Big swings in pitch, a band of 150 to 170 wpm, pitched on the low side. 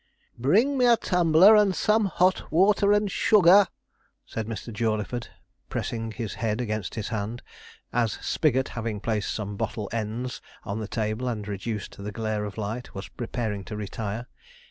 Yes: wide, 7.5 semitones; average, 160 wpm; low, 115 Hz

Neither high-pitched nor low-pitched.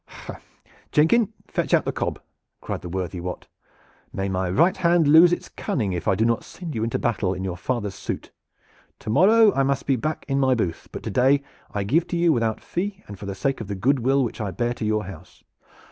No: low, 120 Hz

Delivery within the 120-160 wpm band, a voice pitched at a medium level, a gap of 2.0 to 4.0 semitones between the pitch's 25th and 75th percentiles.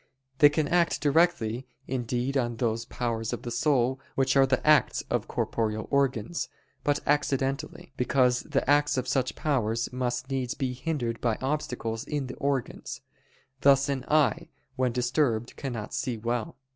No: average, 155 wpm; low, 130 Hz; average, 2.9 semitones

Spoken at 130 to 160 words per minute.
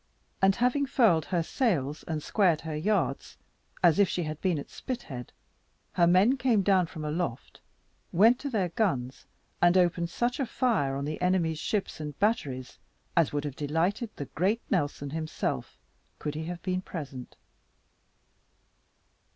Yes: average, 155 wpm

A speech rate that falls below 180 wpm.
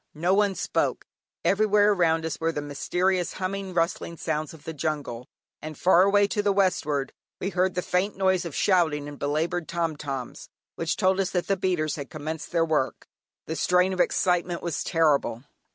No: average, 185 wpm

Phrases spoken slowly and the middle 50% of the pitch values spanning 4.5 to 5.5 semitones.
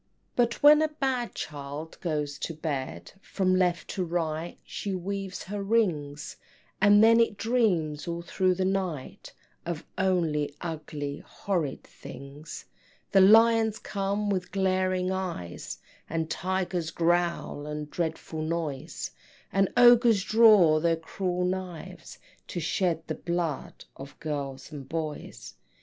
No: slow, 130 wpm; average, 4.1 semitones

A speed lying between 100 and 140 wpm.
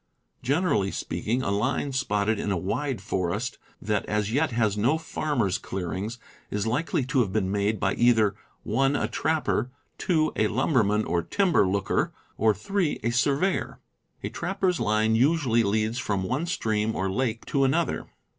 No: average, 155 wpm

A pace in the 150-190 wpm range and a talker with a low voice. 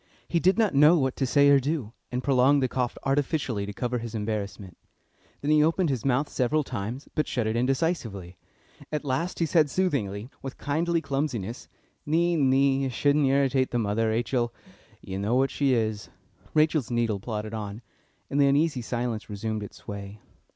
Yes: average, 180 wpm; low, 130 Hz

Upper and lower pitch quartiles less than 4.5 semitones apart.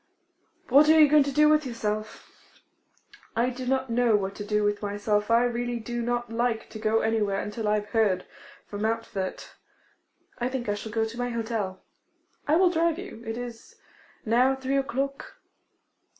Yes: average, 3.4 semitones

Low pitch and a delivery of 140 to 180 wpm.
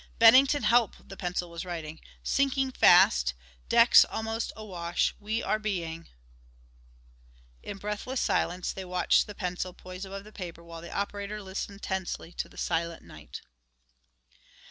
No: high, 190 Hz; average, 145 wpm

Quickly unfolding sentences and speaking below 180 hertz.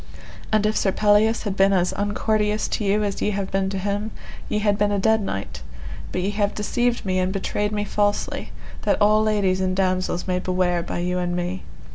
No: fast, 210 wpm; high, 200 Hz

